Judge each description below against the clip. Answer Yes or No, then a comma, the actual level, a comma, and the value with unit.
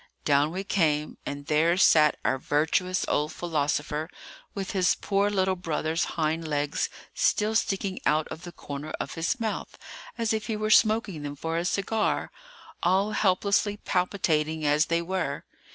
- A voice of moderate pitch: Yes, medium, 170 Hz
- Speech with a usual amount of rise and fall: Yes, average, 4.6 semitones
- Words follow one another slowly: No, average, 155 wpm